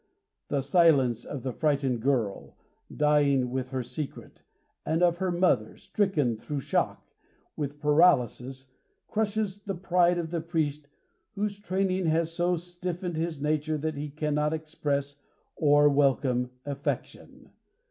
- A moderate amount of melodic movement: Yes, average, 3.8 semitones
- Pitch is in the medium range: Yes, medium, 150 Hz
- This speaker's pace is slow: Yes, slow, 130 wpm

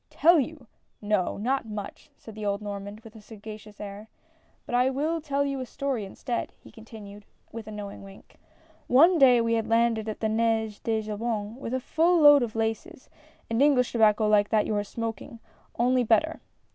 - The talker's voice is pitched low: No, high, 225 Hz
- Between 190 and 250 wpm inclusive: Yes, average, 195 wpm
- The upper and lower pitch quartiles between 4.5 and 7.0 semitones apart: No, average, 3.5 semitones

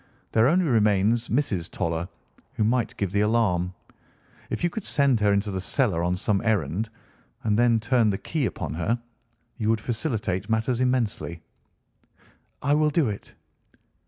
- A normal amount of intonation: Yes, average, 4.0 semitones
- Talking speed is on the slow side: No, average, 160 wpm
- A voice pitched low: Yes, low, 110 Hz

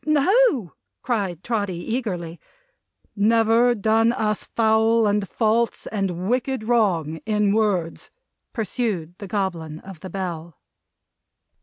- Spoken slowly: Yes, slow, 110 wpm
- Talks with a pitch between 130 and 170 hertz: No, high, 210 Hz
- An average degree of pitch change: Yes, average, 4.1 semitones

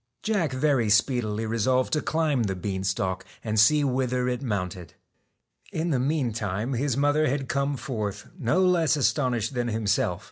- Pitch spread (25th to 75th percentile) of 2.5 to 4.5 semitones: No, average, 5.0 semitones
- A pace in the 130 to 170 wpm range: Yes, average, 155 wpm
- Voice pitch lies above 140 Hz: No, low, 125 Hz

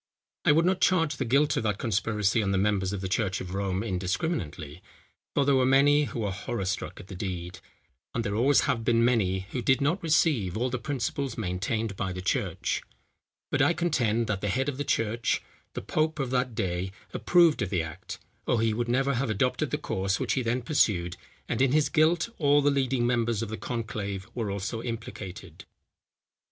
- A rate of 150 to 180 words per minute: No, fast, 205 wpm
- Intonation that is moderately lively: No, wide, 5.8 semitones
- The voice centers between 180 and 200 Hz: No, low, 115 Hz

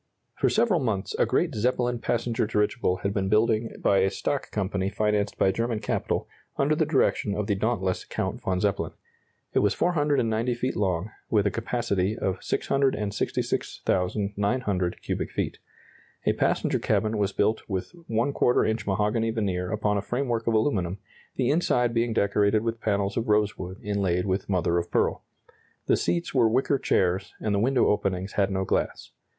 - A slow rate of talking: No, average, 165 wpm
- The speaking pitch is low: Yes, low, 105 Hz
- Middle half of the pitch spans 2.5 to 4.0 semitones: Yes, average, 3.3 semitones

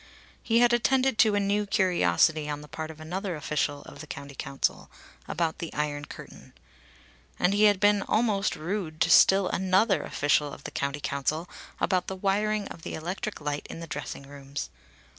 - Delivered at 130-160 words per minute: No, average, 180 wpm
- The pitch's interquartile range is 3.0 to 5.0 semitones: No, wide, 5.6 semitones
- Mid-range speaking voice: Yes, medium, 170 Hz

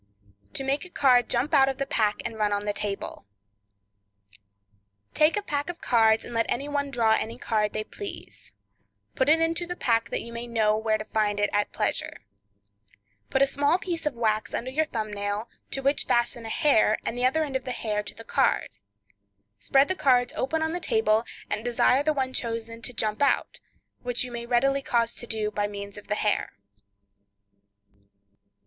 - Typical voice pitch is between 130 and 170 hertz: No, high, 235 Hz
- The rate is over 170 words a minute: Yes, average, 200 wpm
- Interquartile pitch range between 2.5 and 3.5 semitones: No, average, 4.4 semitones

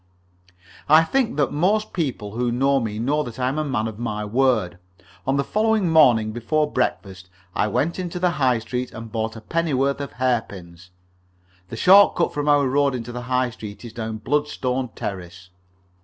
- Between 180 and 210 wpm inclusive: Yes, average, 185 wpm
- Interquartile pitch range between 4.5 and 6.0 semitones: Yes, average, 5.0 semitones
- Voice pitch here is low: Yes, low, 125 Hz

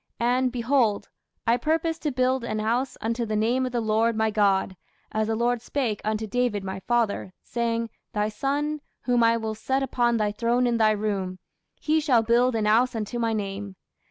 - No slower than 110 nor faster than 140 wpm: No, average, 190 wpm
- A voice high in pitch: Yes, high, 230 Hz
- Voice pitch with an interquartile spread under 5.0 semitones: Yes, narrow, 2.6 semitones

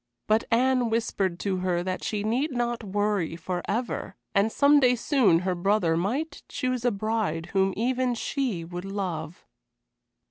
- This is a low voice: No, high, 210 Hz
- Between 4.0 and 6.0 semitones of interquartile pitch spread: Yes, average, 5.0 semitones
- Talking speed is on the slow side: No, average, 150 wpm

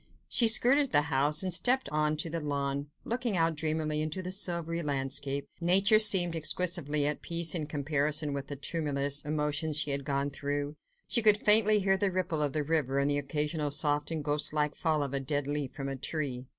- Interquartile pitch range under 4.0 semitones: Yes, average, 3.1 semitones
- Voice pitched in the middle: Yes, medium, 150 Hz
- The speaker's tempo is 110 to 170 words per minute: No, average, 200 wpm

